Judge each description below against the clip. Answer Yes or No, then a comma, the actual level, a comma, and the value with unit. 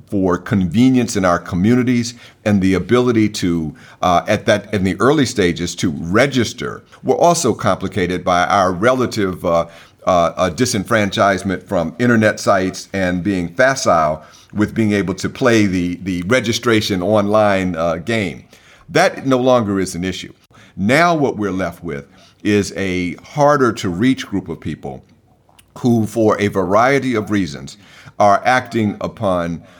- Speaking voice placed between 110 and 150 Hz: No, low, 100 Hz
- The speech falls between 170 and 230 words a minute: No, average, 145 wpm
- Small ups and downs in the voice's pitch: No, average, 4.4 semitones